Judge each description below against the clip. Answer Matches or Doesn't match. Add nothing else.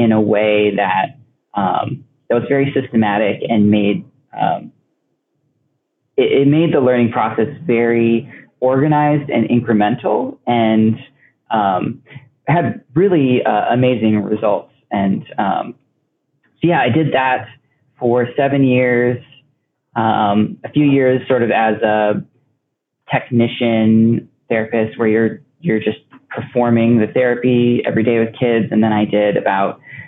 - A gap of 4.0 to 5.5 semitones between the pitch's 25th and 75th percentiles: Doesn't match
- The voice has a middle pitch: Doesn't match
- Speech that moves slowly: Matches